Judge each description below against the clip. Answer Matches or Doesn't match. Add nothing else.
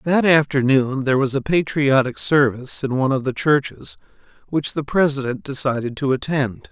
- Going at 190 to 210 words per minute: Doesn't match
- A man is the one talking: Matches